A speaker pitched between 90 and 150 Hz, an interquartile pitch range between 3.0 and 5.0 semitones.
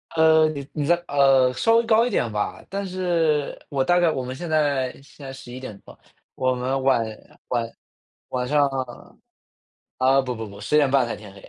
Yes: low, 135 Hz; average, 3.8 semitones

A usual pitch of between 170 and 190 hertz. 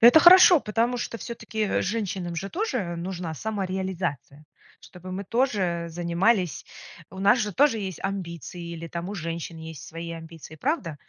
Yes: medium, 185 Hz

